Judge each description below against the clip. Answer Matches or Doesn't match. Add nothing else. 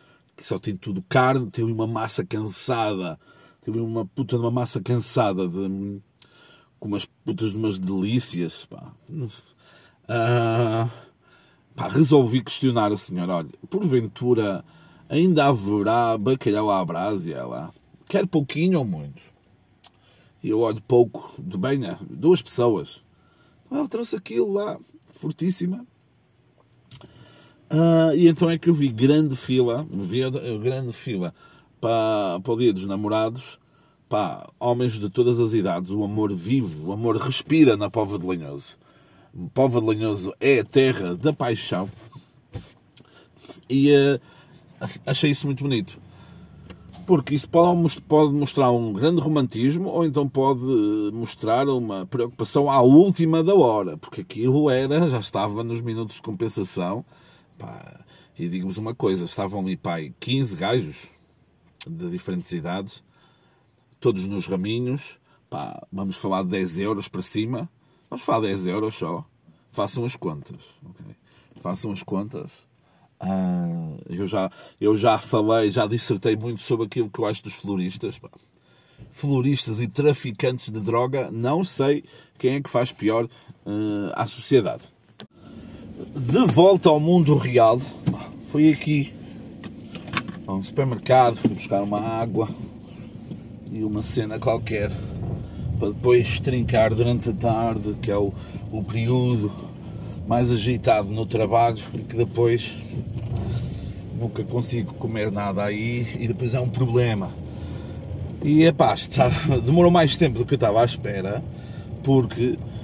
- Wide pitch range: Doesn't match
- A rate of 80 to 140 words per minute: Matches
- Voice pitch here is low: Matches